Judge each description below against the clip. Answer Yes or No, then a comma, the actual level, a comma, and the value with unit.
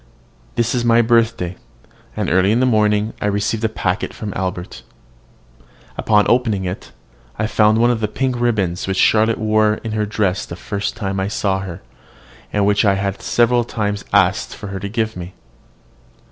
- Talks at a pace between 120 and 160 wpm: No, average, 175 wpm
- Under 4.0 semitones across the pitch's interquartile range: Yes, narrow, 2.6 semitones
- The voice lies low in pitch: Yes, low, 105 Hz